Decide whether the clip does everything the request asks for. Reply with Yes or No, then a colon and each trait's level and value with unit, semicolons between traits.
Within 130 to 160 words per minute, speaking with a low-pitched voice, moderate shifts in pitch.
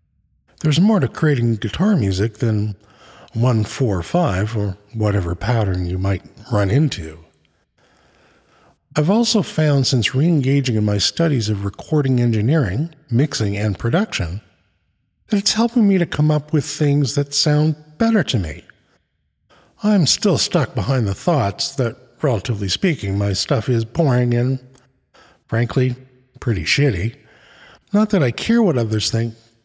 No: average, 140 wpm; low, 125 Hz; wide, 6.4 semitones